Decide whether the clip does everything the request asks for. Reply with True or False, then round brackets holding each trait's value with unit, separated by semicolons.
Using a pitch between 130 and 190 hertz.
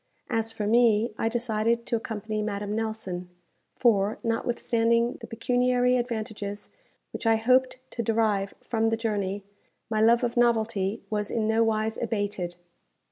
False (225 Hz)